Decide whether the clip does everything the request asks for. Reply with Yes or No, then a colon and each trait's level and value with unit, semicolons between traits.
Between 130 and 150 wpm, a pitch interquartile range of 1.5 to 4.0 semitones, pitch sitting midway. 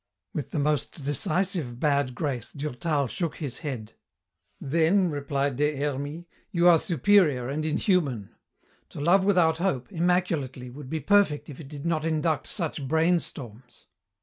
Yes: average, 145 wpm; average, 3.7 semitones; medium, 150 Hz